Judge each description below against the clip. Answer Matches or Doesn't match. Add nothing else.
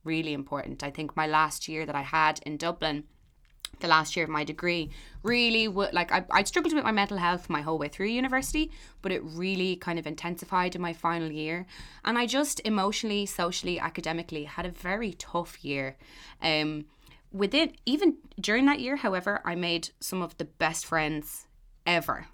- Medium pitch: Matches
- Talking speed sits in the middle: Matches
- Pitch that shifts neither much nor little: Matches